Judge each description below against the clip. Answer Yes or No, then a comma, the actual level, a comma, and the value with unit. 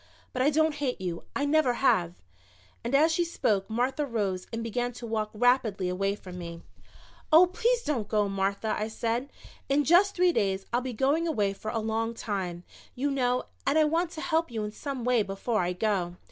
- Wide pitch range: Yes, wide, 6.2 semitones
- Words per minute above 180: Yes, average, 200 wpm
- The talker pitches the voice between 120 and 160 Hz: No, high, 235 Hz